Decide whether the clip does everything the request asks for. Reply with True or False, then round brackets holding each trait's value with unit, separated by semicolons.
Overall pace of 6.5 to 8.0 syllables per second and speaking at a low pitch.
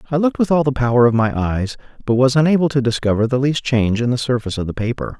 True (7.1 syllables/s; 125 Hz)